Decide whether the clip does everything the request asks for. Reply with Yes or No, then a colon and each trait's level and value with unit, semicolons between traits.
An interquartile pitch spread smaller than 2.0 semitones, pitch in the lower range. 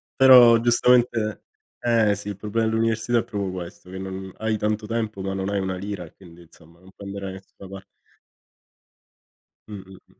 No: average, 2.8 semitones; low, 100 Hz